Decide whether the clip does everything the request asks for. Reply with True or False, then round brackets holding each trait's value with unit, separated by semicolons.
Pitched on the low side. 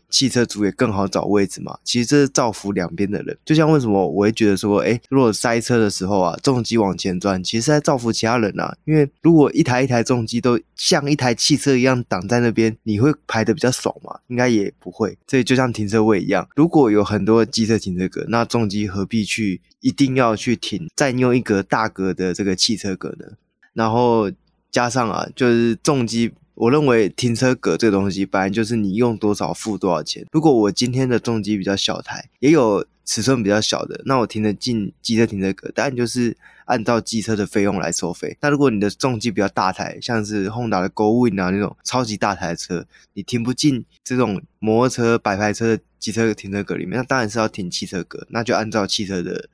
True (115 Hz)